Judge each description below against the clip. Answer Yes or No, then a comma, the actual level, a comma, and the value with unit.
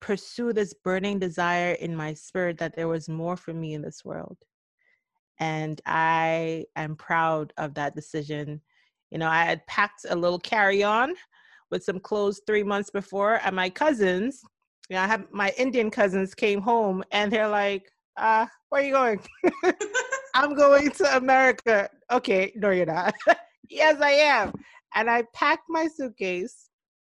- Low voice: No, high, 205 Hz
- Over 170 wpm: No, average, 160 wpm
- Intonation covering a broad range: Yes, wide, 7.0 semitones